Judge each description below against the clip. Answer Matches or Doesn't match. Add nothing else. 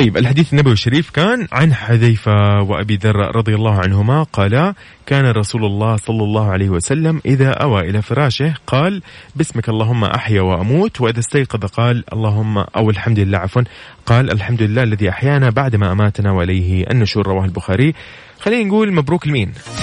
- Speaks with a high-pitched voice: Doesn't match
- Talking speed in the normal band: Doesn't match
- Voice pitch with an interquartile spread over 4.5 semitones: Matches